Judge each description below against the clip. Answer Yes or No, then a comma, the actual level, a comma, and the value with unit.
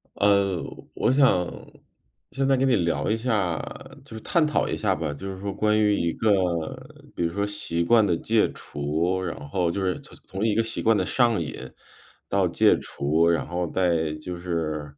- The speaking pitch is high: No, very low, 95 Hz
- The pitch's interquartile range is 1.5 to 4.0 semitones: No, average, 4.4 semitones